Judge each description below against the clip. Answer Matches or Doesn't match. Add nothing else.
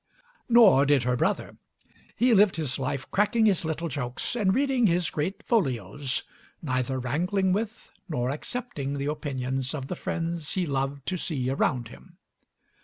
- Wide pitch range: Matches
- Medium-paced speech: Matches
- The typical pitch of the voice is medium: Matches